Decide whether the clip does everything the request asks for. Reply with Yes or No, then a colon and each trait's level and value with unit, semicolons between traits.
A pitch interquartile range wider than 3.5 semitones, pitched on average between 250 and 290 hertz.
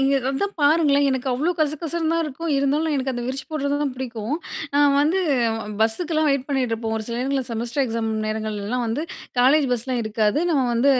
Yes: average, 3.9 semitones; very high, 270 Hz